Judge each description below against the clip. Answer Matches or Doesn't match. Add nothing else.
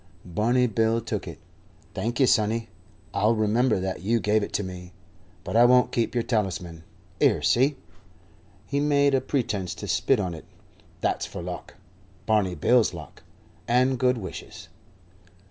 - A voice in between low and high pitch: Doesn't match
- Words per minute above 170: Doesn't match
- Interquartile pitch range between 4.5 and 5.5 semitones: Doesn't match